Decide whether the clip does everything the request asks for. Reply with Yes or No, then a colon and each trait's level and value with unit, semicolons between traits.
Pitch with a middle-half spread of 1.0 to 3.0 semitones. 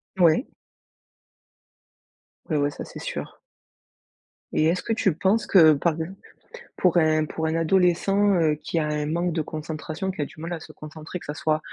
Yes: narrow, 2.5 semitones